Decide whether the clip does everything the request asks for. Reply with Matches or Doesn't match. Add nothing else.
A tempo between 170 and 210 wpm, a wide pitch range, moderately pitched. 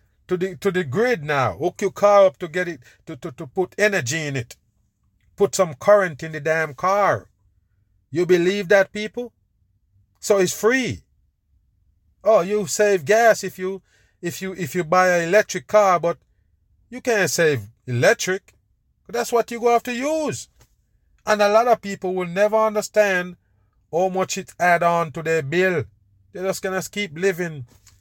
Matches